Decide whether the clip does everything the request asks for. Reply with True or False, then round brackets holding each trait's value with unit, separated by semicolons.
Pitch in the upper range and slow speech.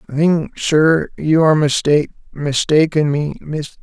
False (150 Hz; 95 wpm)